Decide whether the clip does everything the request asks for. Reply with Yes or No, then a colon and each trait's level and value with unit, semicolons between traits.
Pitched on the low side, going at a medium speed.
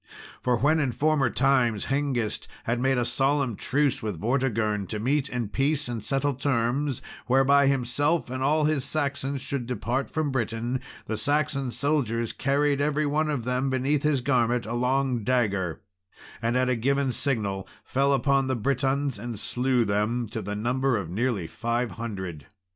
Yes: low, 130 Hz; average, 165 wpm